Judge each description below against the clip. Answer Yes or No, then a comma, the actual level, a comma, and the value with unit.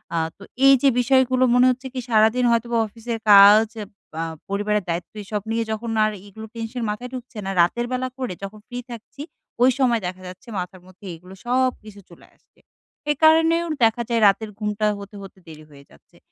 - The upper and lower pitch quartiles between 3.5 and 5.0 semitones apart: Yes, average, 3.8 semitones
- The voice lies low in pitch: No, high, 225 Hz